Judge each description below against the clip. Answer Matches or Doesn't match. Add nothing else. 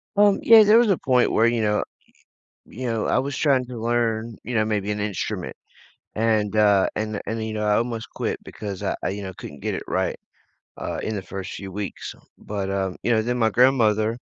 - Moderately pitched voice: Doesn't match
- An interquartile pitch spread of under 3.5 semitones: Matches